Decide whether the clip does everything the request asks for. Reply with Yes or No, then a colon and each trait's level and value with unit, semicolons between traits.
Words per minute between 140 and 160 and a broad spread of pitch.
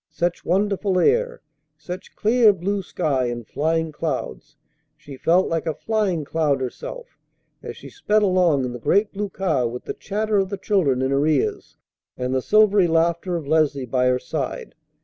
No: average, 175 wpm; wide, 6.2 semitones